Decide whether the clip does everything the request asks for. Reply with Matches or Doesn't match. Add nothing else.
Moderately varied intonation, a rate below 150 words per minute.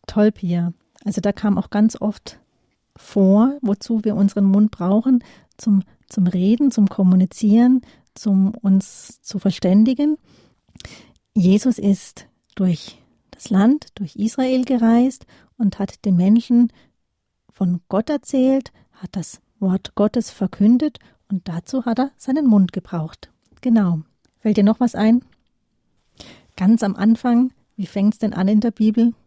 Matches